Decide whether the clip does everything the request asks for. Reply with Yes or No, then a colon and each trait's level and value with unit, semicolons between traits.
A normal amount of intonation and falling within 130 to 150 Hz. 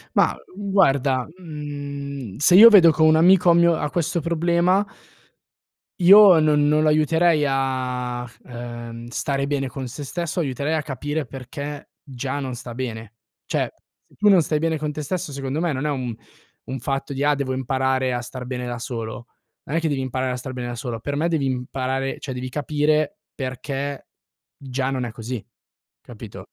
Yes: average, 3.4 semitones; medium, 140 Hz